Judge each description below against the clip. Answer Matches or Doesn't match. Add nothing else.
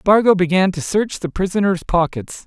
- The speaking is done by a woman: Doesn't match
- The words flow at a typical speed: Matches